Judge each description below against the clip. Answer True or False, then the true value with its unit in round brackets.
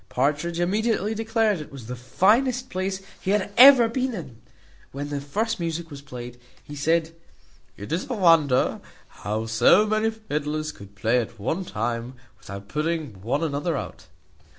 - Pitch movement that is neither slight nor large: False (8.7 semitones)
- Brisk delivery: False (160 wpm)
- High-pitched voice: False (155 Hz)